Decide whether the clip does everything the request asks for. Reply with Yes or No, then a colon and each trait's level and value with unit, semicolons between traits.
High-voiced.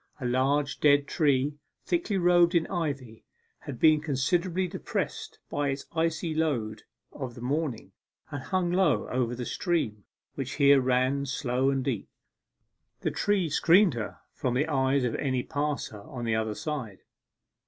No: medium, 140 Hz